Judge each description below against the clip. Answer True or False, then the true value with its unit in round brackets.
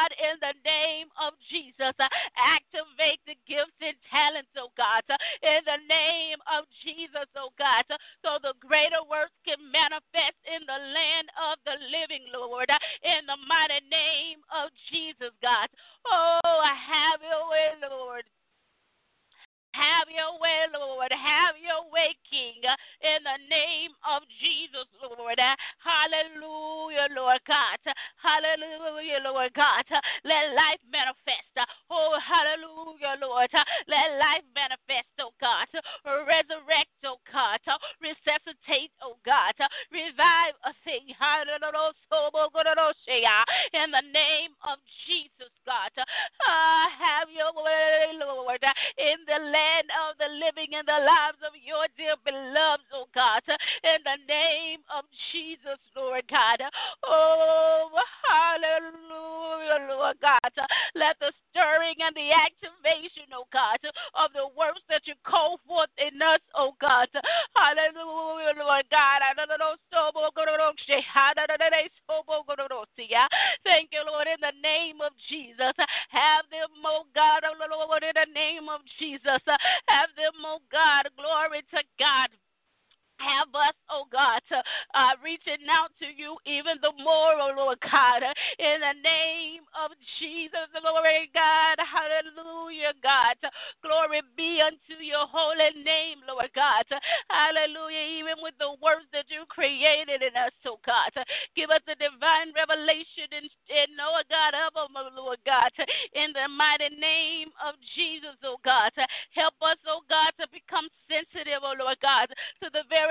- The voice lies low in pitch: False (305 Hz)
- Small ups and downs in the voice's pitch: True (2.1 semitones)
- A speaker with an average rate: False (130 wpm)